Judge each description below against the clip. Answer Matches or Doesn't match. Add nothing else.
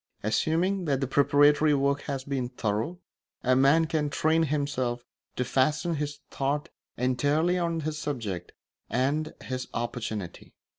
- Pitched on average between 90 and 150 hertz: Matches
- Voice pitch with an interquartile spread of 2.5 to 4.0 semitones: Matches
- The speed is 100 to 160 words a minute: Matches